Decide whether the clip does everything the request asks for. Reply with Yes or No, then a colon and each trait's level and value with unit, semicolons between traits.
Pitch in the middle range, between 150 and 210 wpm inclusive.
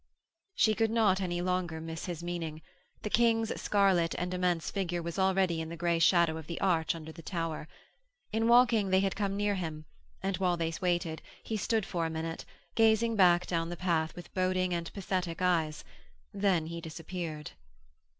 Yes: medium, 175 Hz; average, 180 wpm